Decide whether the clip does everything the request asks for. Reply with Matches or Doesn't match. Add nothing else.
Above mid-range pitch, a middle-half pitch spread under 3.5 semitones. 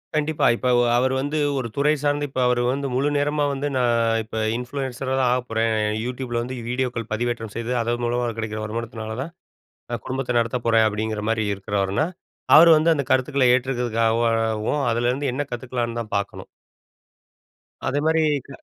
Doesn't match